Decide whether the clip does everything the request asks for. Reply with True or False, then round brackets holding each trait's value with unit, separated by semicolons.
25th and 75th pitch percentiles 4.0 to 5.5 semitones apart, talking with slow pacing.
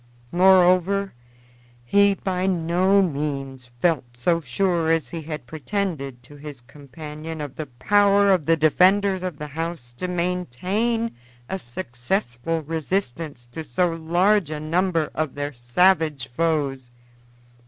True (4.5 semitones; 130 wpm)